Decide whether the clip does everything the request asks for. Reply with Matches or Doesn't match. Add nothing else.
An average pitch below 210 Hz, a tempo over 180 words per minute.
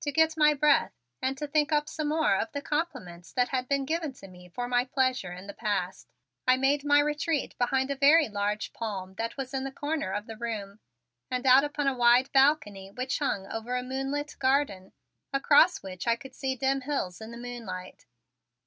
Doesn't match